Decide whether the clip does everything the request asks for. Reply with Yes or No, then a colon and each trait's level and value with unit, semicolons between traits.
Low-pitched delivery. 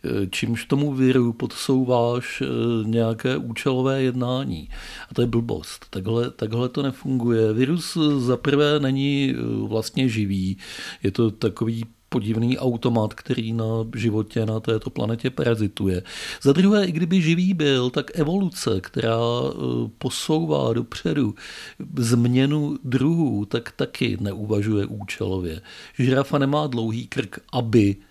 Yes: low, 120 Hz